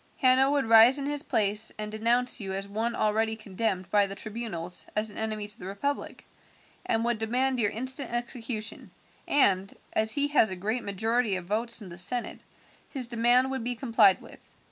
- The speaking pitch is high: Yes, high, 225 Hz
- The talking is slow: No, average, 190 wpm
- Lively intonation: No, average, 3.2 semitones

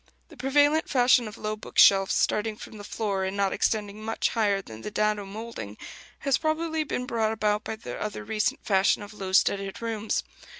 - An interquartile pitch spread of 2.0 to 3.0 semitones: Yes, narrow, 2.6 semitones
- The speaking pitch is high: Yes, high, 215 Hz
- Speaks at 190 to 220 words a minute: Yes, average, 195 wpm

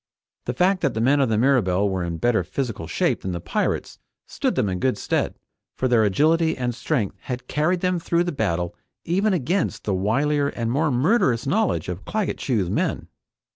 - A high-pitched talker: No, low, 130 Hz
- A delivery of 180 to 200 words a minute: Yes, average, 195 wpm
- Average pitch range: No, wide, 7.7 semitones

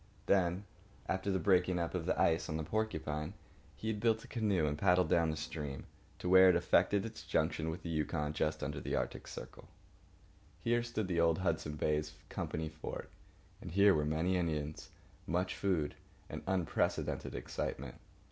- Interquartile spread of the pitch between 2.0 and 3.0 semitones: No, average, 3.5 semitones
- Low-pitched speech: Yes, very low, 85 Hz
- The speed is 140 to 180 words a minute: Yes, average, 175 wpm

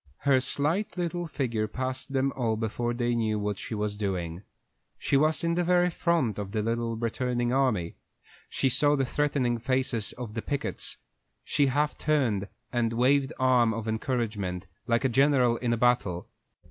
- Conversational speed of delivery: Yes, average, 170 wpm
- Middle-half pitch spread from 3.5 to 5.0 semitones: Yes, average, 3.8 semitones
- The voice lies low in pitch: Yes, low, 120 Hz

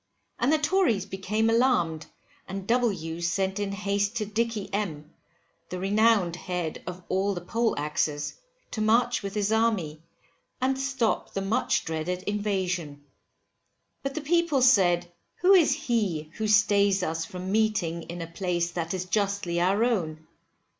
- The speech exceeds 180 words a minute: No, average, 145 wpm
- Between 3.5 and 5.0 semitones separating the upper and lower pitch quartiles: Yes, average, 4.6 semitones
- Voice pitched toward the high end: Yes, high, 200 Hz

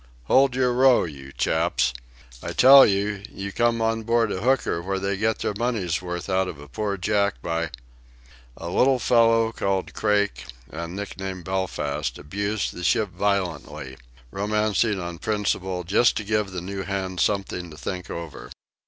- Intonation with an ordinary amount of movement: Yes, average, 3.6 semitones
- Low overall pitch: Yes, low, 100 Hz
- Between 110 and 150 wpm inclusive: No, average, 160 wpm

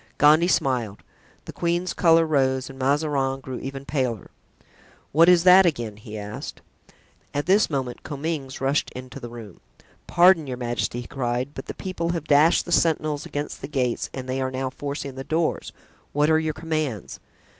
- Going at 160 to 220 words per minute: Yes, average, 175 wpm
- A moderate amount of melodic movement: Yes, average, 3.7 semitones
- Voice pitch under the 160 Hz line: Yes, medium, 140 Hz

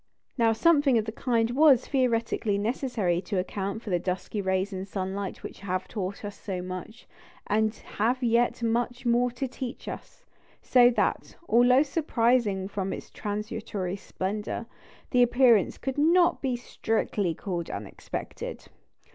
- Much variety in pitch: No, average, 4.1 semitones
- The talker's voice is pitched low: No, high, 225 Hz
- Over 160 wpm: No, average, 145 wpm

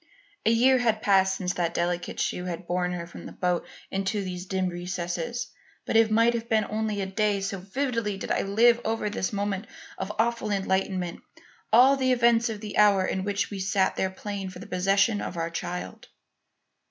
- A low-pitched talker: No, high, 200 Hz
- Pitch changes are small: No, average, 3.4 semitones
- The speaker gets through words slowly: No, average, 200 wpm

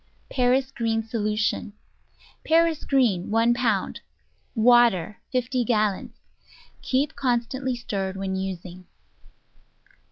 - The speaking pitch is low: No, high, 230 Hz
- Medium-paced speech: No, slow, 90 wpm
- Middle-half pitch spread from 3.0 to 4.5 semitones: Yes, average, 4.1 semitones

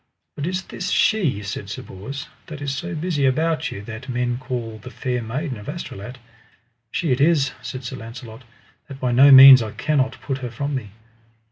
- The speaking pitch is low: Yes, low, 130 Hz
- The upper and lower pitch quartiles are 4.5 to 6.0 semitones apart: No, average, 3.4 semitones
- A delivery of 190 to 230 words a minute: Yes, average, 195 wpm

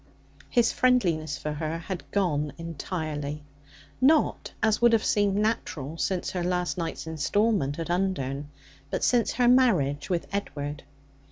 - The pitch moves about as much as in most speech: No, wide, 5.9 semitones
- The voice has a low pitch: No, medium, 175 Hz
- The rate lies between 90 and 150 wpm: Yes, average, 140 wpm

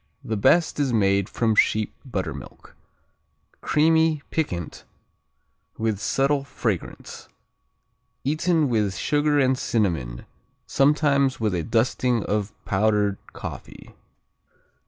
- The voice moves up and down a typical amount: No, wide, 6.2 semitones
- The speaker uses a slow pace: Yes, slow, 95 wpm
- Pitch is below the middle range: Yes, low, 115 Hz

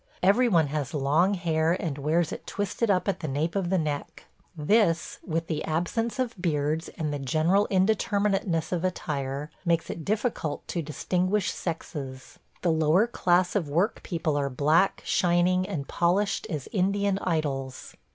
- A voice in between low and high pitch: Yes, medium, 170 Hz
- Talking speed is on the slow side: No, average, 160 wpm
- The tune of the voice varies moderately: Yes, average, 4.1 semitones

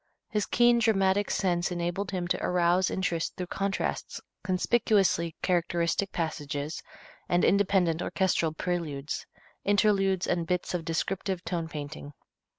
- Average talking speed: No, slow, 120 wpm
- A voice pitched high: No, medium, 180 Hz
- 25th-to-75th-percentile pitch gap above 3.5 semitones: No, narrow, 2.6 semitones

